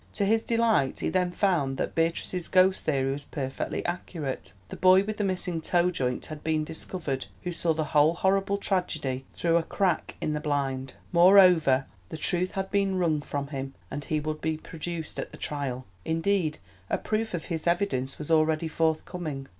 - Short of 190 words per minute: Yes, average, 180 wpm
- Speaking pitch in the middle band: Yes, medium, 160 Hz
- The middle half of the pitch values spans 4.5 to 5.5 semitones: No, average, 4.1 semitones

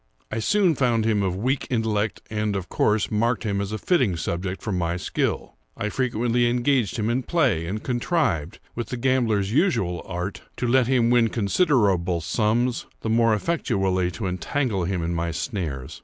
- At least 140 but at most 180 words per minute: Yes, average, 175 wpm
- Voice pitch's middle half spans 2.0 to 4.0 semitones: No, average, 4.7 semitones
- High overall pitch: No, low, 110 Hz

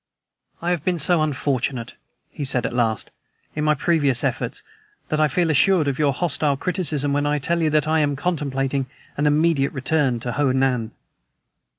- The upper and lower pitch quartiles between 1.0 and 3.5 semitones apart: Yes, average, 2.9 semitones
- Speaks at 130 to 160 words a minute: No, average, 180 wpm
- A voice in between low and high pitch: Yes, medium, 145 Hz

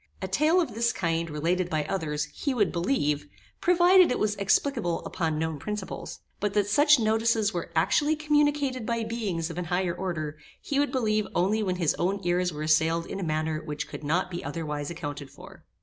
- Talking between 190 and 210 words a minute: Yes, average, 195 wpm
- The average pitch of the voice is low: No, medium, 185 Hz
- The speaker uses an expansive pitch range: Yes, wide, 6.3 semitones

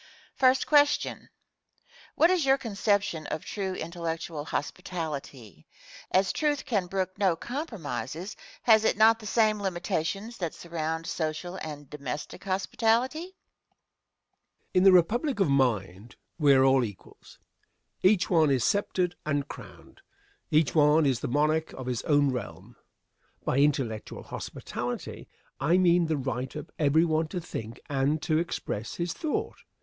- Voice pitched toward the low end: No, medium, 165 Hz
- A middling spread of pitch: No, wide, 5.8 semitones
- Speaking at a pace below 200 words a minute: Yes, average, 140 wpm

